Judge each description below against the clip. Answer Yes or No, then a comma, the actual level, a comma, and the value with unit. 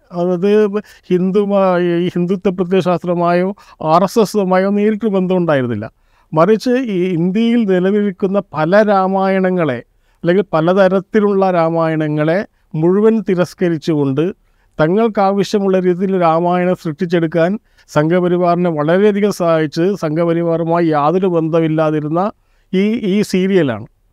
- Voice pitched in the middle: Yes, medium, 180 Hz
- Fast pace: No, average, 85 wpm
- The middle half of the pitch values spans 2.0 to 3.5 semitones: Yes, average, 3.1 semitones